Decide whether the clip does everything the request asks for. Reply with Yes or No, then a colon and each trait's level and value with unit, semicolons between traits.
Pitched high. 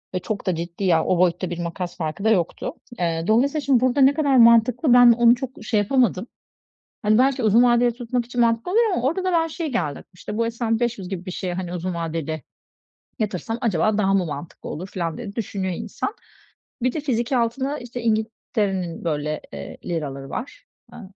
Yes: high, 220 Hz